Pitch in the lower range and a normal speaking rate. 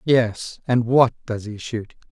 Yes: low, 115 Hz; average, 170 wpm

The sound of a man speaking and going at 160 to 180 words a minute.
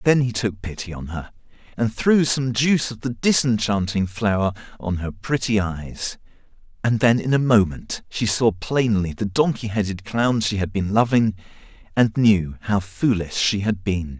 Yes: male; average, 175 wpm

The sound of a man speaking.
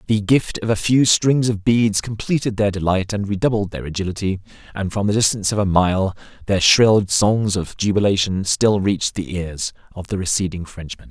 Yes: male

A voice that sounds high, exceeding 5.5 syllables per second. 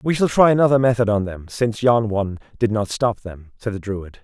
No: low, 110 Hz; 5.8 syllables/s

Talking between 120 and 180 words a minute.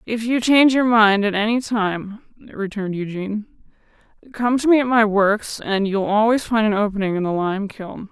No: average, 190 wpm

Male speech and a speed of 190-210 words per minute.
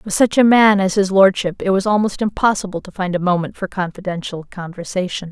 No: female; fast, 205 wpm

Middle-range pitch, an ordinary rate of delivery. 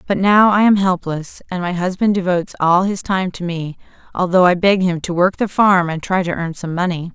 No: medium, 180 Hz; fast, 235 wpm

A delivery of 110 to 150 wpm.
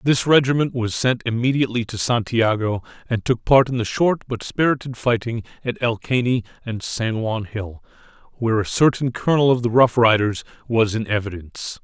No: average, 165 wpm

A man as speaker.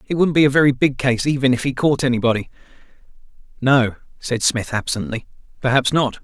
Yes: male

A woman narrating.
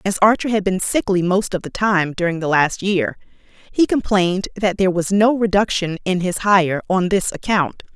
Yes: female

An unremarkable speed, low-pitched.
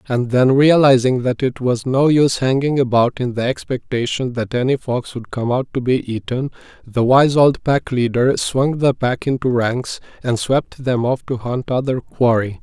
Yes: average, 190 wpm; low, 125 Hz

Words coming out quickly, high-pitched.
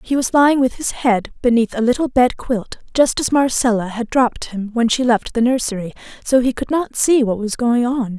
Yes: fast, 225 wpm; high, 240 Hz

